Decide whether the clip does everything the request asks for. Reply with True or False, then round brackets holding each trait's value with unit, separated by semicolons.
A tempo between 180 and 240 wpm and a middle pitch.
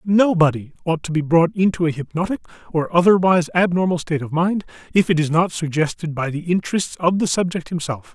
True (190 wpm; 170 Hz)